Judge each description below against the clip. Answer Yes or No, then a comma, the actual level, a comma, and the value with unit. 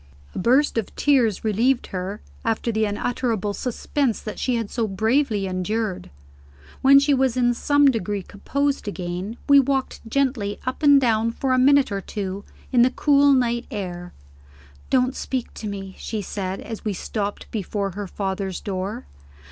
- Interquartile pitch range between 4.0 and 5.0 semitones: Yes, average, 4.4 semitones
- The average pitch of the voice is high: Yes, high, 225 Hz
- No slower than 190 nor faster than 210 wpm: No, average, 165 wpm